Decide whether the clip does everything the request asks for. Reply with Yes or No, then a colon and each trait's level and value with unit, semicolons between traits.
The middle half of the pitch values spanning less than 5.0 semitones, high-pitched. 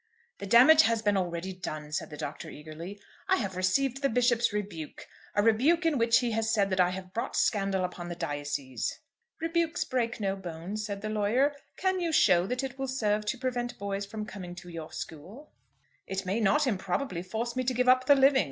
No: wide, 5.5 semitones; high, 210 Hz